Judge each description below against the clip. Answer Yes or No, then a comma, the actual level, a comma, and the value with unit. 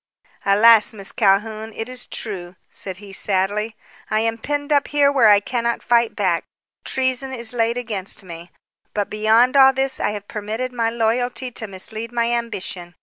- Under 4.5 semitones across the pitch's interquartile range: Yes, average, 3.1 semitones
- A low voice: No, high, 225 Hz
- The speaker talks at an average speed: Yes, average, 170 wpm